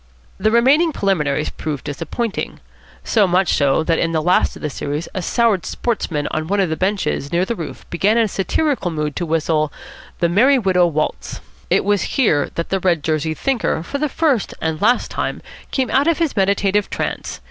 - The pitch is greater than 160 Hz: Yes, medium, 185 Hz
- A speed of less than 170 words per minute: No, average, 190 wpm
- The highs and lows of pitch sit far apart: Yes, wide, 6.3 semitones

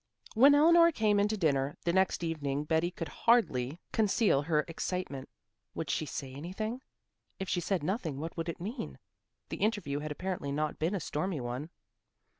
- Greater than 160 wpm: Yes, average, 175 wpm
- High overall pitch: No, medium, 170 Hz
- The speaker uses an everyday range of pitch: No, wide, 5.7 semitones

